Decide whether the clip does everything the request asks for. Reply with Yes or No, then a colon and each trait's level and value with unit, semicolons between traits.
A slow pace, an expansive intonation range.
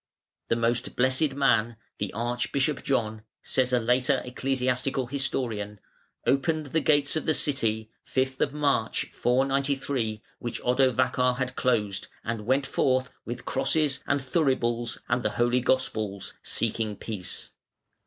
No: slow, 125 wpm; average, 2.8 semitones